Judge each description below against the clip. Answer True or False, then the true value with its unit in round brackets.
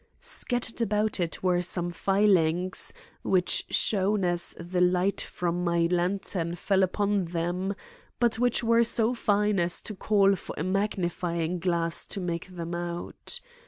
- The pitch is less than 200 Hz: True (185 Hz)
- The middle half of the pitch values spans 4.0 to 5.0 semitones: False (2.9 semitones)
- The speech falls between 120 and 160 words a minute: True (145 wpm)